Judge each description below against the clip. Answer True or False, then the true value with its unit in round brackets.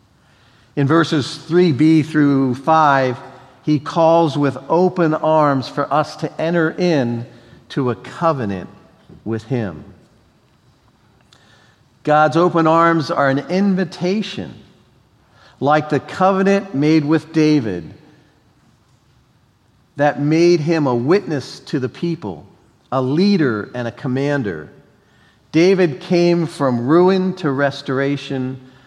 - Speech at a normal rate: False (105 wpm)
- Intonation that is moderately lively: True (4.1 semitones)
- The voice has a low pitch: False (145 Hz)